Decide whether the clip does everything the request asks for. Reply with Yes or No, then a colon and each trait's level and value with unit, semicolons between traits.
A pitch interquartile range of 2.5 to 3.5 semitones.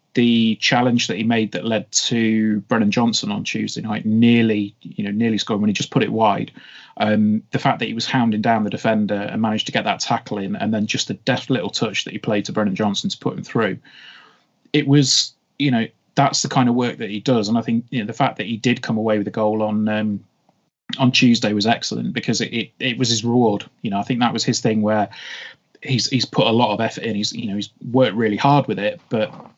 Yes: average, 3.2 semitones